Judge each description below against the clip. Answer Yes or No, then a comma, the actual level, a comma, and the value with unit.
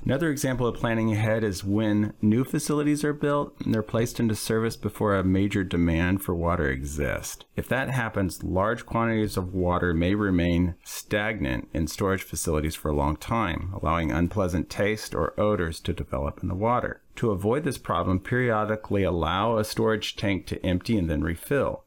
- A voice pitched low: Yes, low, 100 Hz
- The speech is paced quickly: No, average, 175 wpm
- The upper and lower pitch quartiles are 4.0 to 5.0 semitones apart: Yes, average, 4.6 semitones